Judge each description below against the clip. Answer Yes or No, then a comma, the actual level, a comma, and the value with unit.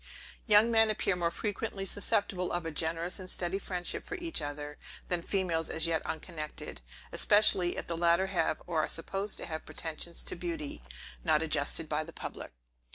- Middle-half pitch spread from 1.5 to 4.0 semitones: Yes, average, 3.2 semitones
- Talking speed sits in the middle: Yes, average, 175 wpm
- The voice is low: No, medium, 170 Hz